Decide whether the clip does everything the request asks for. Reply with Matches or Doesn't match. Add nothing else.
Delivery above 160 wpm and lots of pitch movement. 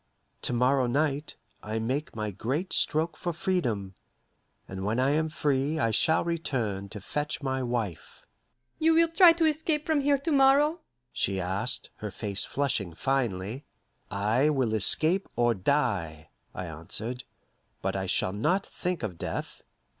Doesn't match